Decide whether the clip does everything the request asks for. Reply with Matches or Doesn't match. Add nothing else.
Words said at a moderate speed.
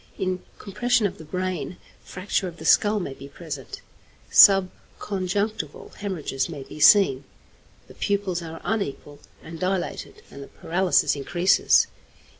Doesn't match